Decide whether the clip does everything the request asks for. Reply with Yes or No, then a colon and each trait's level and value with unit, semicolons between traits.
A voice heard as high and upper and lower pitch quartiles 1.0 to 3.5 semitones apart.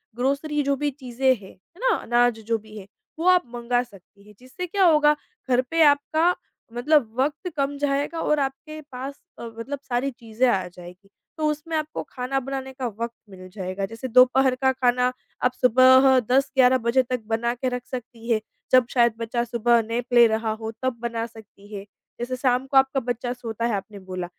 Yes: very high, 250 Hz; average, 3.0 semitones